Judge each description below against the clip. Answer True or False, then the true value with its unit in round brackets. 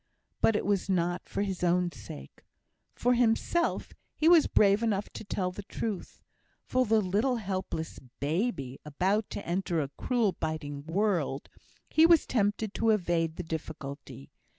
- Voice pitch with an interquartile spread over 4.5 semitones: True (5.2 semitones)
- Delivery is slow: False (150 wpm)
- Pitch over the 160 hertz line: True (190 Hz)